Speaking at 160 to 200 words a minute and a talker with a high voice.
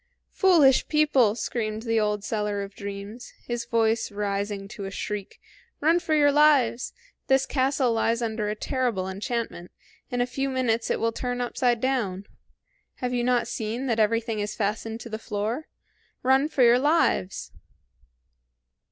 No: average, 150 wpm; high, 230 Hz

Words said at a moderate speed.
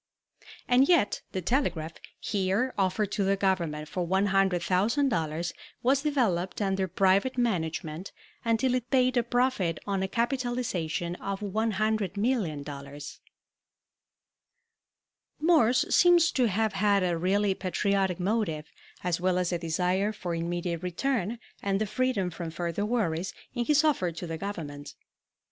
No: slow, 130 wpm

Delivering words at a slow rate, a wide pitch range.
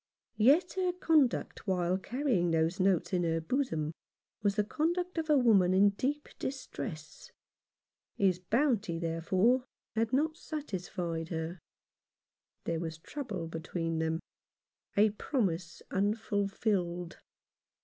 Yes: slow, 120 wpm; wide, 7.2 semitones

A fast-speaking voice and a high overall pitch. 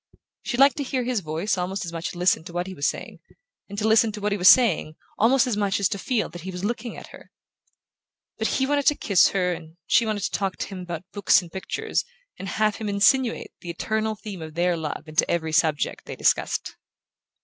Yes: fast, 240 wpm; high, 195 Hz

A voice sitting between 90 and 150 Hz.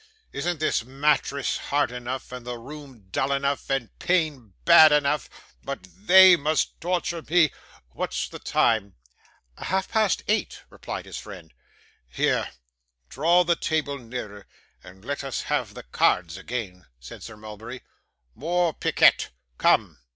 Yes: low, 135 Hz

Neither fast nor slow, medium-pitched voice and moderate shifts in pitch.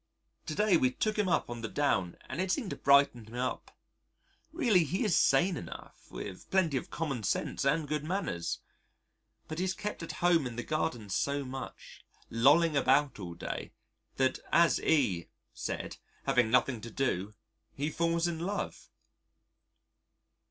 No: average, 160 wpm; medium, 145 Hz; wide, 5.8 semitones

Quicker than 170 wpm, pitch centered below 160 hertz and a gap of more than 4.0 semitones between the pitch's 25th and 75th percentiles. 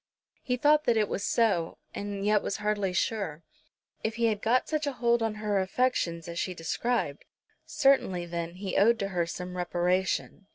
No: average, 180 wpm; high, 205 Hz; average, 4.6 semitones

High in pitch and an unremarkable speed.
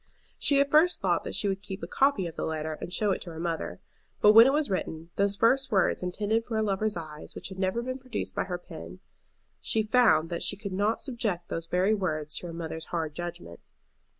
No: high, 195 Hz; fast, 230 wpm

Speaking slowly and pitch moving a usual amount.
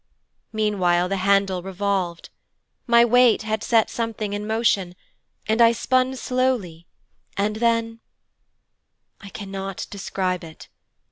Yes: slow, 115 wpm; average, 3.2 semitones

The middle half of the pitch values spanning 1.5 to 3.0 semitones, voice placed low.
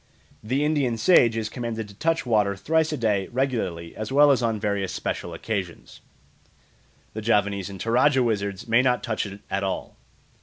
No: average, 4.2 semitones; low, 110 Hz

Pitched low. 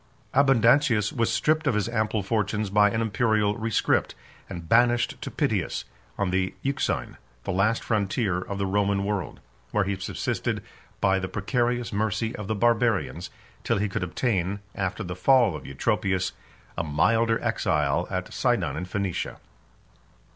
Yes: low, 105 Hz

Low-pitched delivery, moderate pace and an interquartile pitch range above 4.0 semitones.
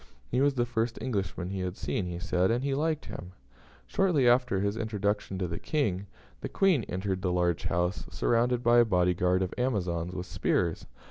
Yes: low, 100 Hz; average, 195 wpm; average, 5.3 semitones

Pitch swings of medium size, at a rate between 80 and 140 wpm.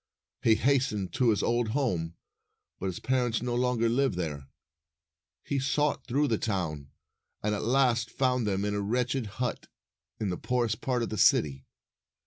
No: average, 4.0 semitones; average, 165 wpm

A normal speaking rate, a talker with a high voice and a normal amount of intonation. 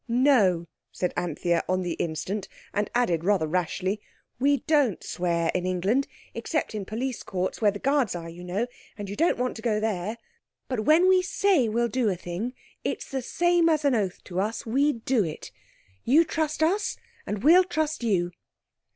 No: average, 175 wpm; high, 220 Hz; wide, 7.2 semitones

